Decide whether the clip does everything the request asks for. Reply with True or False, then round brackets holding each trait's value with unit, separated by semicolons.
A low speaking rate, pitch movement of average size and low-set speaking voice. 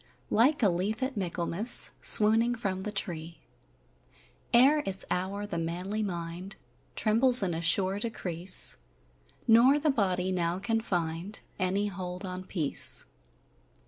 False (130 wpm; 3.8 semitones; 195 Hz)